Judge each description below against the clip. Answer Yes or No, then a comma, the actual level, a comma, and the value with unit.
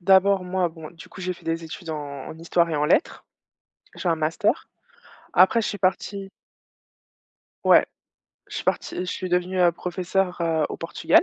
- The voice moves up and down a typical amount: No, narrow, 2.3 semitones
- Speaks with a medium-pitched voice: Yes, medium, 180 Hz